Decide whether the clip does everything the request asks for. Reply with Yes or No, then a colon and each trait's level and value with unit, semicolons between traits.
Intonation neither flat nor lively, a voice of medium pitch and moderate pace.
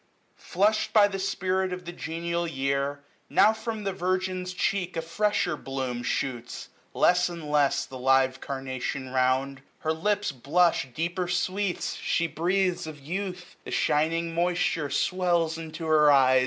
Yes: average, 4.8 semitones; medium, 170 Hz; average, 150 wpm